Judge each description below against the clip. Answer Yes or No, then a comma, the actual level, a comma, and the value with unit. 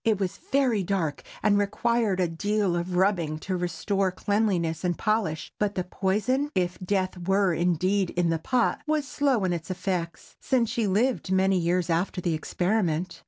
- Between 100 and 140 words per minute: No, average, 165 wpm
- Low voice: No, high, 190 Hz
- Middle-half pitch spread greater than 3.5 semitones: No, average, 3.2 semitones